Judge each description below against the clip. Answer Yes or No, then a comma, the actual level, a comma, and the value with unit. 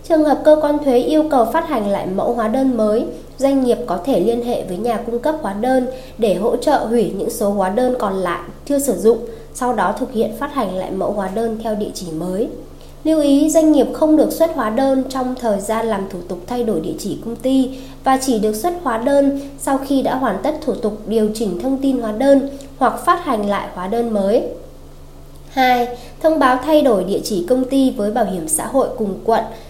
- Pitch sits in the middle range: No, high, 240 Hz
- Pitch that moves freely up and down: No, average, 4.1 semitones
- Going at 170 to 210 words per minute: No, average, 235 wpm